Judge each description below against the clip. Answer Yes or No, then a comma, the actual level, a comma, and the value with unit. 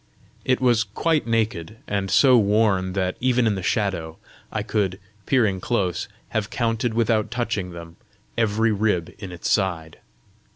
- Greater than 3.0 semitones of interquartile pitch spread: Yes, average, 3.7 semitones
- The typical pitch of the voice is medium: No, low, 105 Hz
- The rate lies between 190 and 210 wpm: No, average, 150 wpm